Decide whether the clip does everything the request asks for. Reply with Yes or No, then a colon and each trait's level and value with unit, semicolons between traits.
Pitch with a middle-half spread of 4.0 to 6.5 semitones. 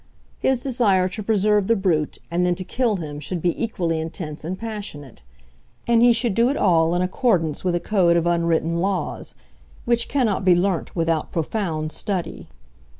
Yes: average, 4.5 semitones